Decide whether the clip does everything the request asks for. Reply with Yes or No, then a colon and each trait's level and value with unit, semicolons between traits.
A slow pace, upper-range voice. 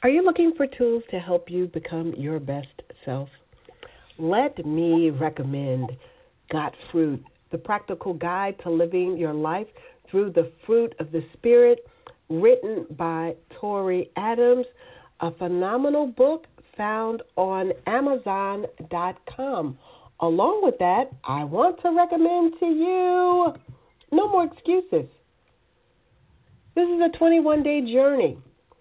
Yes: slow, 120 wpm; high, 200 Hz